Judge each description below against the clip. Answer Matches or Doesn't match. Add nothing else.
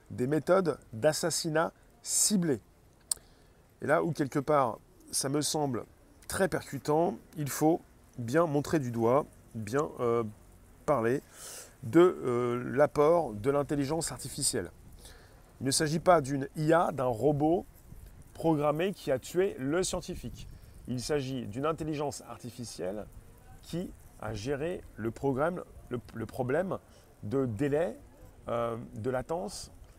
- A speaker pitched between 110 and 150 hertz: Matches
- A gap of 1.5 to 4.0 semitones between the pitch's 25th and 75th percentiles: Doesn't match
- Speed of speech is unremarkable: Doesn't match